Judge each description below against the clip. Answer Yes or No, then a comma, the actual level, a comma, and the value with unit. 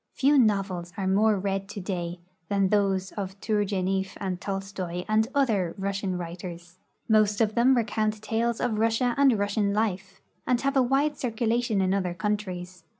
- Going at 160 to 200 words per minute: Yes, average, 165 wpm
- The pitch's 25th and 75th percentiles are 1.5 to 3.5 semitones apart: Yes, average, 2.9 semitones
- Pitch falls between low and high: No, high, 200 Hz